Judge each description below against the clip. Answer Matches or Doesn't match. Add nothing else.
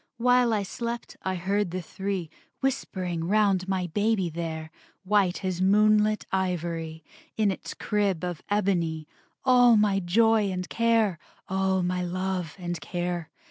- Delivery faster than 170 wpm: Doesn't match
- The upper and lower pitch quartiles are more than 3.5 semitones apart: Doesn't match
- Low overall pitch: Doesn't match